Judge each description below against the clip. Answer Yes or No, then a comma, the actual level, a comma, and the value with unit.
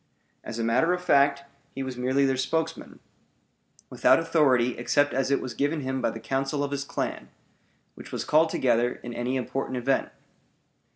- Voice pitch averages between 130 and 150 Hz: Yes, low, 135 Hz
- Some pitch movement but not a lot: No, narrow, 2.3 semitones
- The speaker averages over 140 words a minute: Yes, average, 175 wpm